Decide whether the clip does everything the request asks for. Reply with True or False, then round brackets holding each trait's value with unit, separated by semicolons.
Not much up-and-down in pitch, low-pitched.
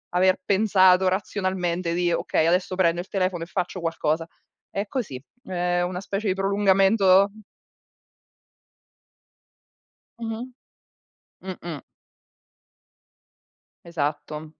False (2.3 semitones; 185 Hz)